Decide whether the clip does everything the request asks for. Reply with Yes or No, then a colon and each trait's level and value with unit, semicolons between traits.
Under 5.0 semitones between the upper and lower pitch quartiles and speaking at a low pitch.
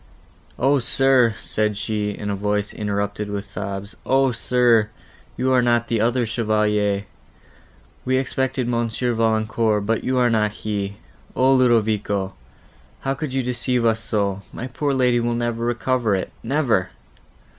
Yes: average, 3.2 semitones; low, 115 Hz